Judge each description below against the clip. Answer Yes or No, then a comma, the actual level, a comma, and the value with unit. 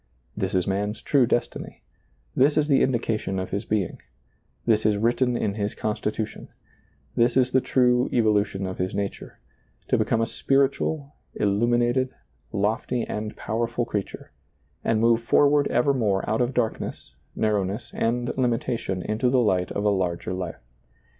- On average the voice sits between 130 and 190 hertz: No, low, 115 Hz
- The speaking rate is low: No, average, 155 wpm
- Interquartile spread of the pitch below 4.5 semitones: Yes, average, 3.3 semitones